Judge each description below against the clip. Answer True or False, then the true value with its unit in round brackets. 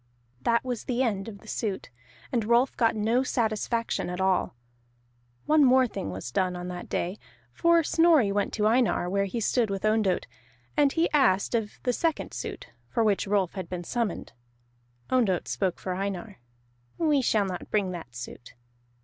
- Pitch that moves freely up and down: False (4.8 semitones)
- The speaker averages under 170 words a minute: False (175 wpm)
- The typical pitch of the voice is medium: False (215 Hz)